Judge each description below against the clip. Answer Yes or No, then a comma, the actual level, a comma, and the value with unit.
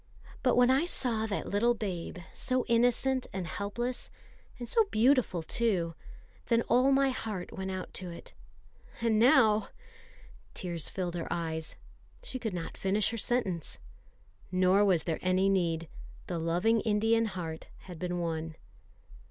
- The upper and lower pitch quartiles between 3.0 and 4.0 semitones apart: No, average, 5.2 semitones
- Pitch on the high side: Yes, high, 200 Hz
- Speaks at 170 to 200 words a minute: No, average, 150 wpm